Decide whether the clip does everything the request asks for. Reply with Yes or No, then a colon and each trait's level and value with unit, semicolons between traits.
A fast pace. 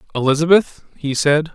No: slow, 115 wpm